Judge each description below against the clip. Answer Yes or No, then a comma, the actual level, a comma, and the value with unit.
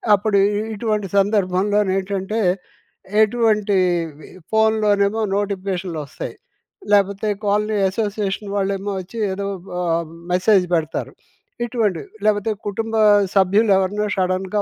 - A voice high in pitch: Yes, high, 200 Hz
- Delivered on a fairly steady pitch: Yes, narrow, 1.9 semitones